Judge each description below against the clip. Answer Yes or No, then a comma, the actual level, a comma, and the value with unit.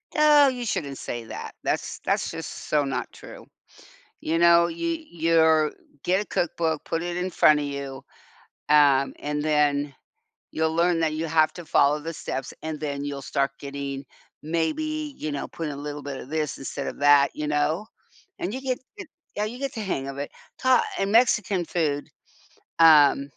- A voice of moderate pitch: Yes, medium, 155 Hz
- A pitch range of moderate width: Yes, average, 3.6 semitones